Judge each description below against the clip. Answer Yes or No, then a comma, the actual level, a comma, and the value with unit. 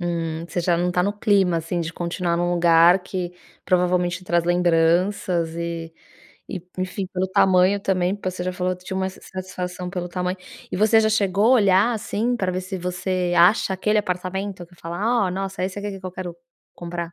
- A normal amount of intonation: No, narrow, 1.6 semitones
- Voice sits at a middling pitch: Yes, medium, 180 Hz